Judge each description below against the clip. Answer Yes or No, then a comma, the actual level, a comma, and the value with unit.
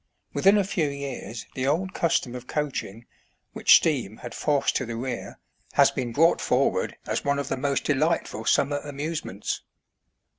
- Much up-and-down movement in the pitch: No, average, 3.8 semitones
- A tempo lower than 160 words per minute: No, average, 170 wpm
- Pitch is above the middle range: No, medium, 140 Hz